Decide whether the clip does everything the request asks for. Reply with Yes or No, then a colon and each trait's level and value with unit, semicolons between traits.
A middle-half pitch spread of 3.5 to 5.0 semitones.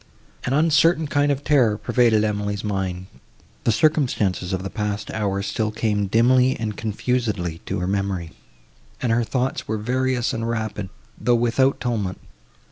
Yes: average, 3.8 semitones